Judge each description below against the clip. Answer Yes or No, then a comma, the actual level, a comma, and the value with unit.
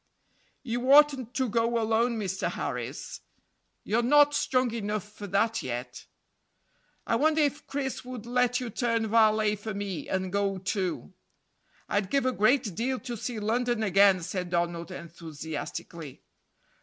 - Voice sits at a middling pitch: No, high, 220 Hz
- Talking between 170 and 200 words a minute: No, average, 145 wpm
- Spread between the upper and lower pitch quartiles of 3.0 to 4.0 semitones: No, average, 4.4 semitones